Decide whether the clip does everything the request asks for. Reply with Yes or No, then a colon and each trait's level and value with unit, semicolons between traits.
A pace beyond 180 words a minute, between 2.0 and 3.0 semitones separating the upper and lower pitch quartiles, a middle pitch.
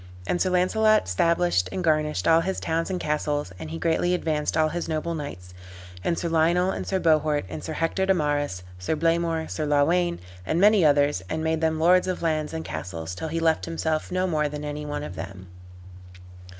Yes: average, 200 wpm; average, 2.7 semitones; medium, 160 Hz